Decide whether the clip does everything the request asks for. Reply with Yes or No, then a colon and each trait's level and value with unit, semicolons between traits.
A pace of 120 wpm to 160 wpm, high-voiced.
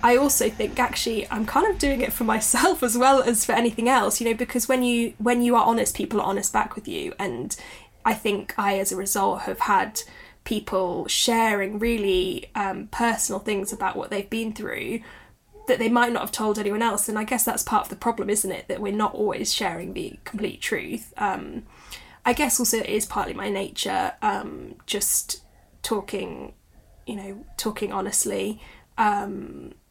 No: average, 190 wpm; high, 225 Hz